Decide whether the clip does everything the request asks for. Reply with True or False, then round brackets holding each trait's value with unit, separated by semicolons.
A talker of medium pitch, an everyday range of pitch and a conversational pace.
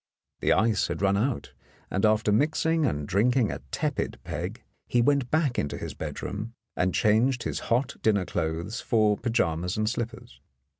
False (110 Hz; 3.7 semitones; 160 wpm)